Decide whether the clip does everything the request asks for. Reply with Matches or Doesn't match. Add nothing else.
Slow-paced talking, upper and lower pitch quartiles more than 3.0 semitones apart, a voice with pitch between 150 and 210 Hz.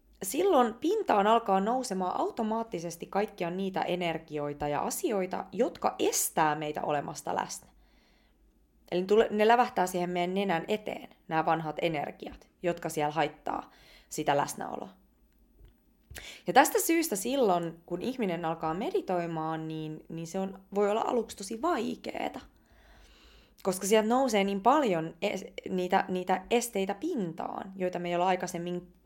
Doesn't match